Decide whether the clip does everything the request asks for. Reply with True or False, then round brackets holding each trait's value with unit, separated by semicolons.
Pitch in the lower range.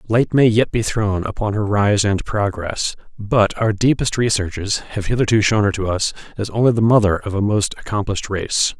True (105 Hz)